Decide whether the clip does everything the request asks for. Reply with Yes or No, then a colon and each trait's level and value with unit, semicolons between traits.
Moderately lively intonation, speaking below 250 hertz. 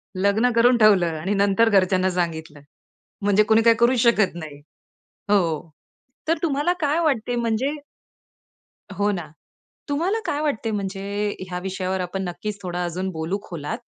Yes: average, 4.6 semitones; high, 200 Hz